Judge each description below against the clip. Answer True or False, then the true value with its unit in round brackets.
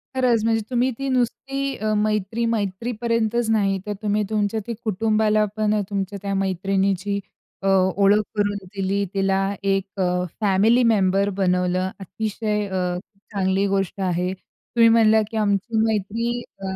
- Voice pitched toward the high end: True (205 Hz)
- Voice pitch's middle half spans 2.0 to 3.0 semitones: True (2.5 semitones)